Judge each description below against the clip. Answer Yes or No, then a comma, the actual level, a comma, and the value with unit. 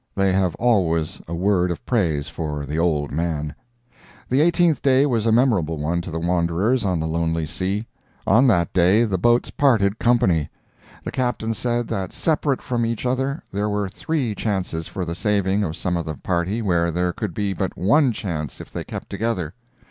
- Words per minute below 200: Yes, average, 190 wpm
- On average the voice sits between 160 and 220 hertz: No, very low, 95 Hz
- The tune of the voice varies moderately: No, wide, 5.7 semitones